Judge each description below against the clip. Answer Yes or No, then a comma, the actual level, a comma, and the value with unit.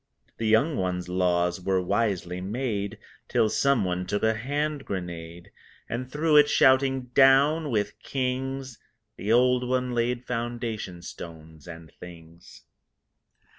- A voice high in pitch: No, low, 115 Hz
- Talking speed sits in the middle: No, slow, 125 wpm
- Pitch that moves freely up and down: Yes, wide, 6.4 semitones